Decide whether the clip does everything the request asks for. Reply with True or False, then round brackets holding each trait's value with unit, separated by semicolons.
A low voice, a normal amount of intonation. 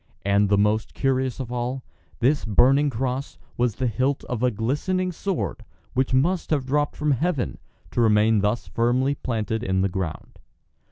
True (125 Hz; 4.0 semitones)